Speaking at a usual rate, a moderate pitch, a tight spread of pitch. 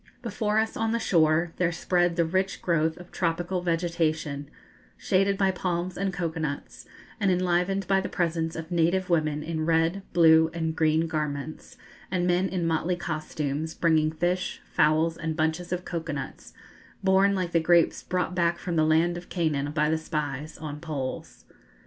Yes: average, 170 wpm; medium, 170 Hz; narrow, 2.3 semitones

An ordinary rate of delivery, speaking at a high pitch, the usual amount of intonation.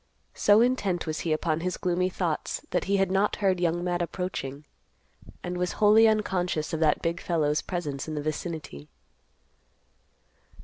No: average, 160 wpm; medium, 175 Hz; average, 3.3 semitones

